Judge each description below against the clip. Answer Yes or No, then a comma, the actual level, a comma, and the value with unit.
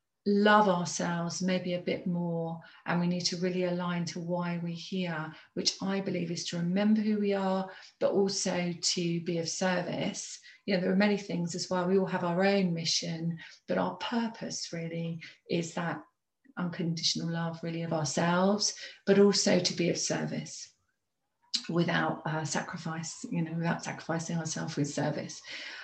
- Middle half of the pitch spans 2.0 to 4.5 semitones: Yes, narrow, 2.4 semitones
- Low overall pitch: No, medium, 175 Hz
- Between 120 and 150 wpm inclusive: No, average, 165 wpm